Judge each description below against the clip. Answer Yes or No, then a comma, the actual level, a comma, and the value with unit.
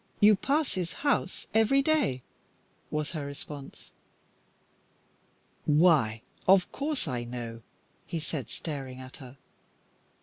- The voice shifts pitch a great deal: Yes, wide, 8.3 semitones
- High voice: No, medium, 155 Hz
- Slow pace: Yes, slow, 110 wpm